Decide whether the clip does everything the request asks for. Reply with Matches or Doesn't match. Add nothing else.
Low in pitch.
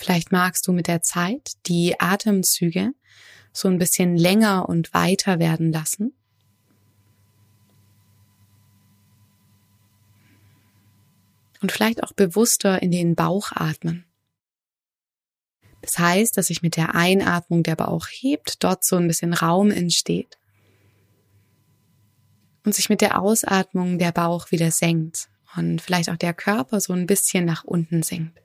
Doesn't match